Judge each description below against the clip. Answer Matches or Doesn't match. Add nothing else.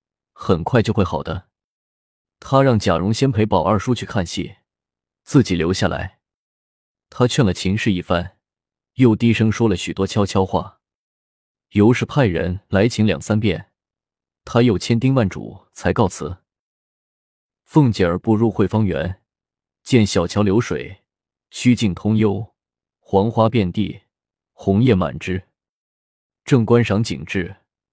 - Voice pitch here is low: Matches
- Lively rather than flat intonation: Doesn't match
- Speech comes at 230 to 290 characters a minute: Doesn't match